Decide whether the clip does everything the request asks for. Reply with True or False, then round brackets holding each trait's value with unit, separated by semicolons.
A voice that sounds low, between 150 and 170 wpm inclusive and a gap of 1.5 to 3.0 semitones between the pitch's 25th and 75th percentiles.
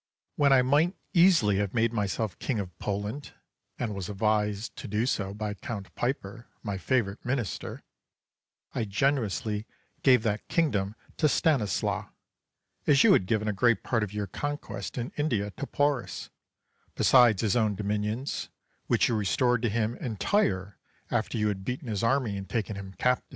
False (110 Hz; 165 wpm; 3.9 semitones)